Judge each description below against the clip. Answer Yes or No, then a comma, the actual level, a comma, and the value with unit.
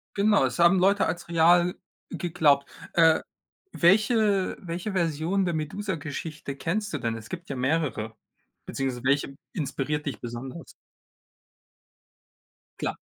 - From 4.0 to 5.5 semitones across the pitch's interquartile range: Yes, average, 4.7 semitones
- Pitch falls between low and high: Yes, medium, 165 Hz